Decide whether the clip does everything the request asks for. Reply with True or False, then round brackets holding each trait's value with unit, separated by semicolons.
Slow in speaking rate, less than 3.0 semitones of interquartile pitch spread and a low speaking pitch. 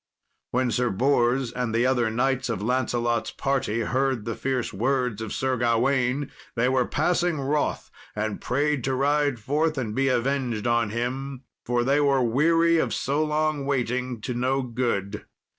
False (160 wpm; 2.6 semitones; 130 Hz)